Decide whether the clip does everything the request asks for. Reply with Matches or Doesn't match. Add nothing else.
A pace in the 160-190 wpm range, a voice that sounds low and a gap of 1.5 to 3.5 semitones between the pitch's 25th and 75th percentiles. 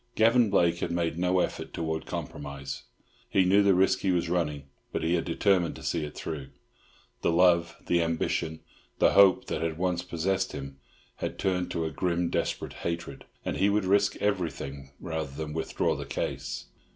Matches